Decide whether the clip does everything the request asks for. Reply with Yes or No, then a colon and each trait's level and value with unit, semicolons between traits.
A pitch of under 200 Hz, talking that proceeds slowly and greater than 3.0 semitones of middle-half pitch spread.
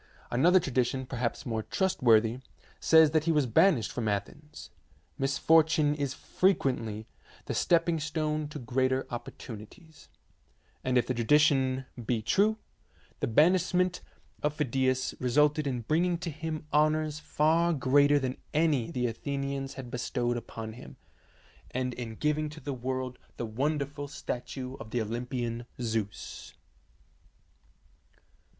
Yes: low, 135 Hz; slow, 130 wpm; average, 4.1 semitones